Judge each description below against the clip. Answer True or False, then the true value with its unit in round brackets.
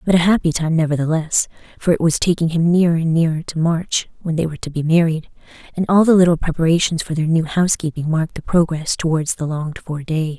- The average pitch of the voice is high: False (165 Hz)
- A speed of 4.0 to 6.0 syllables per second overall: False (6.2 syllables/s)